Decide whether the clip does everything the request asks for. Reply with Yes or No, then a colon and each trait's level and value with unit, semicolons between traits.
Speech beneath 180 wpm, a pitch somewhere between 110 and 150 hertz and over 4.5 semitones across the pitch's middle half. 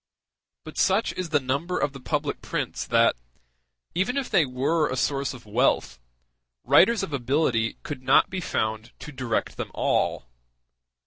Yes: average, 155 wpm; medium, 140 Hz; average, 5.3 semitones